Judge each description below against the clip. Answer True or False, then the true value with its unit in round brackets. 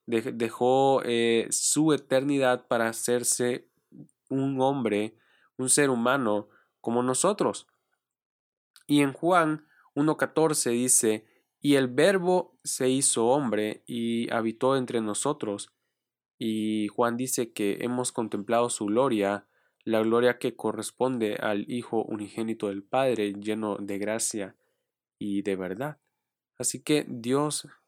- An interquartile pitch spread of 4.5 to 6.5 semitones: False (3.7 semitones)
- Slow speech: True (115 wpm)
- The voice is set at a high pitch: False (120 Hz)